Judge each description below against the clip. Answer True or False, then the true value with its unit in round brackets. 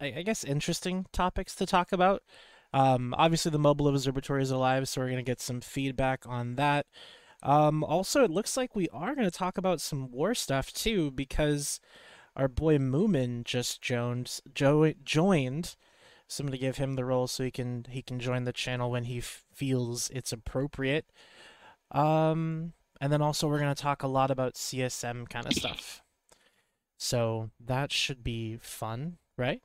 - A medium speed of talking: True (160 wpm)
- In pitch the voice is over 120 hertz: True (140 Hz)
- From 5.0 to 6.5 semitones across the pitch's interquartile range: False (3.9 semitones)